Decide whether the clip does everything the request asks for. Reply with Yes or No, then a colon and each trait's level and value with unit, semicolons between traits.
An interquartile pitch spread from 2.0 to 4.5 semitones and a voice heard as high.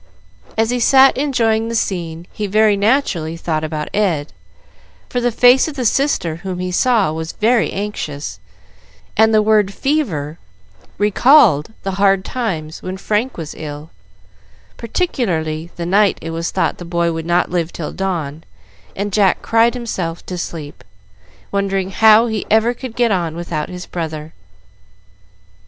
No: average, 5.3 semitones; high, 195 Hz